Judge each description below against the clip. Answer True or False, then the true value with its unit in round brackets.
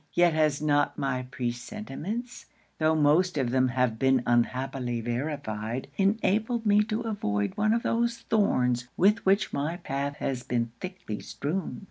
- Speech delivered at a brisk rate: False (150 wpm)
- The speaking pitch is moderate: True (145 Hz)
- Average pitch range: False (8.1 semitones)